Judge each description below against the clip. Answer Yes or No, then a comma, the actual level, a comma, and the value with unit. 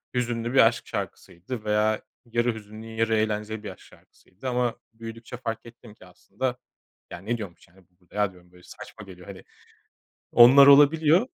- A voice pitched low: Yes, low, 110 Hz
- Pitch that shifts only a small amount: No, average, 3.0 semitones